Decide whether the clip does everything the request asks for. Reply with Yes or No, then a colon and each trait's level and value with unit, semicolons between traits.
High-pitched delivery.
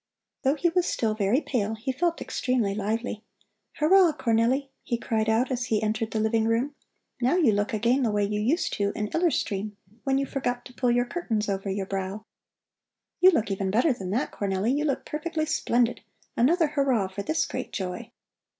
Yes: high, 235 Hz